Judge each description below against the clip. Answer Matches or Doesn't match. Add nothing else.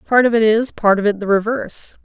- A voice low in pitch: Doesn't match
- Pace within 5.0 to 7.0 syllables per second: Matches